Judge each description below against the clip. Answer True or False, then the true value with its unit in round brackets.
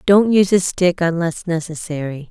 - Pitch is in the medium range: True (175 Hz)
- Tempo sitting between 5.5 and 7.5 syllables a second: False (5.0 syllables/s)